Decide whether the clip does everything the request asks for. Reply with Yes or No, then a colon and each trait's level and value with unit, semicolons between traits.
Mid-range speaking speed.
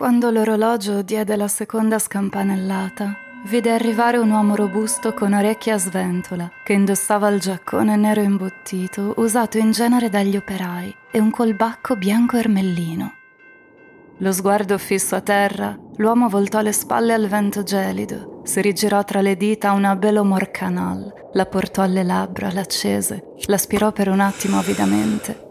Yes: average, 145 wpm